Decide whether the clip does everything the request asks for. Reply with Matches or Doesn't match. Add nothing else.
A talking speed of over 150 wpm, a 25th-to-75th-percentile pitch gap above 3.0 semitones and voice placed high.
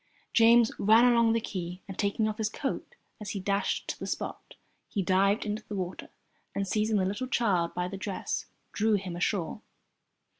Doesn't match